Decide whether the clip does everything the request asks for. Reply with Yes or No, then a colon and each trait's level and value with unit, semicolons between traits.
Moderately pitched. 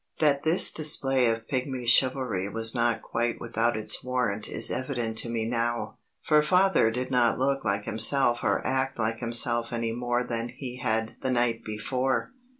No: low, 120 Hz